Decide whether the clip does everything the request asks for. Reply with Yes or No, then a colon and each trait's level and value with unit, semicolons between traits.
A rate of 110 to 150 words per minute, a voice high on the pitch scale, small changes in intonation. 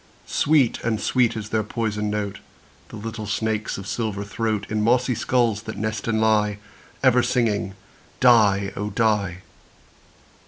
No: average, 145 wpm; low, 110 Hz; narrow, 1.9 semitones